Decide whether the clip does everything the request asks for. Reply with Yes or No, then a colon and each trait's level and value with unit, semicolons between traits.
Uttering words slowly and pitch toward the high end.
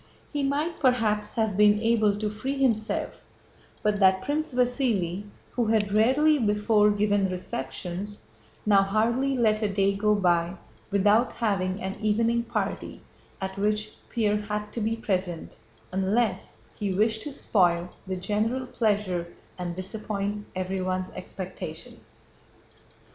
Yes: slow, 130 wpm; high, 210 Hz